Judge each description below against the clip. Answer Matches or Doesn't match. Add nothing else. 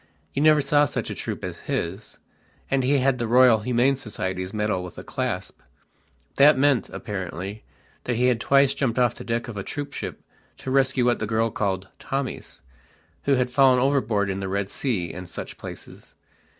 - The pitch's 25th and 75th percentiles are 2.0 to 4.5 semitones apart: Doesn't match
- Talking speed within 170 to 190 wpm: Matches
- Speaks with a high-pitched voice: Doesn't match